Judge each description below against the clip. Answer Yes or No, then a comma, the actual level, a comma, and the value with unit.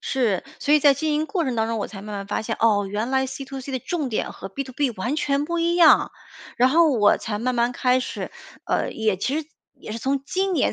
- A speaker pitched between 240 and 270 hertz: Yes, very high, 260 Hz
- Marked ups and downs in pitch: No, average, 4.8 semitones